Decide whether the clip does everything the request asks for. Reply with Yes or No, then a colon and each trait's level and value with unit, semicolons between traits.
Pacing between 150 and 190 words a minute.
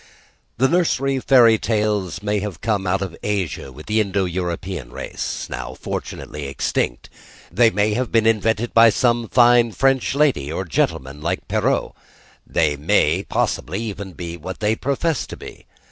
Yes: average, 160 wpm